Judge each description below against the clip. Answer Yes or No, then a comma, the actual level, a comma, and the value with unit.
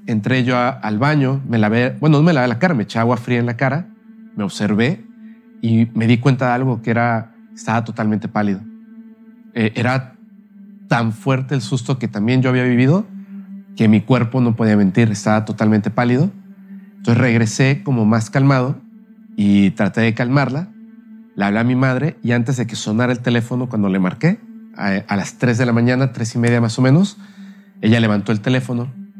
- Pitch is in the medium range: No, low, 125 Hz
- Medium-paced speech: No, fast, 195 wpm